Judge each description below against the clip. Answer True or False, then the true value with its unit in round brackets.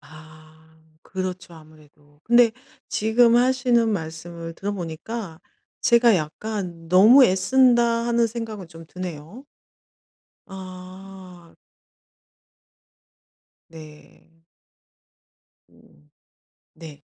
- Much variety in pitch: True (5.9 semitones)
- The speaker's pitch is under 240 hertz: True (185 Hz)